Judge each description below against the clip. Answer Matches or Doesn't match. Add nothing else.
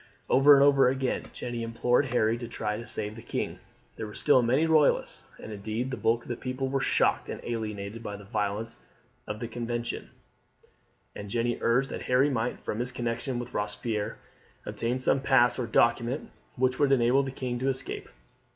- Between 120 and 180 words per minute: Doesn't match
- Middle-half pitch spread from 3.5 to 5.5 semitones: Doesn't match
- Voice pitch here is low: Matches